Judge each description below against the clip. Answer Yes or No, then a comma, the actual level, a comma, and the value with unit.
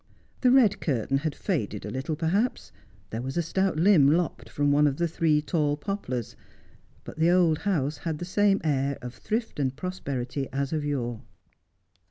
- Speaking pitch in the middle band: Yes, medium, 150 Hz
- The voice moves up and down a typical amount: Yes, average, 4.7 semitones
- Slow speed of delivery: No, average, 180 wpm